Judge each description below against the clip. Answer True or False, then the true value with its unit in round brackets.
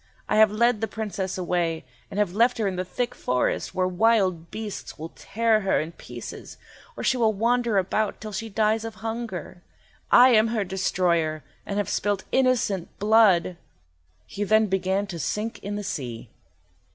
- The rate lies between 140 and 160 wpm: False (175 wpm)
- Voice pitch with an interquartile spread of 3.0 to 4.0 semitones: True (3.3 semitones)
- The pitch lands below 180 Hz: False (205 Hz)